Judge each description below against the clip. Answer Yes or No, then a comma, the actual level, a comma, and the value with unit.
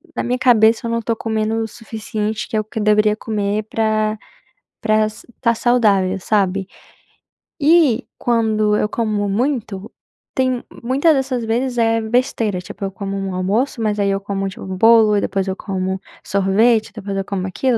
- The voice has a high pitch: Yes, high, 215 Hz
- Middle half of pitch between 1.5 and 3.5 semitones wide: Yes, average, 2.7 semitones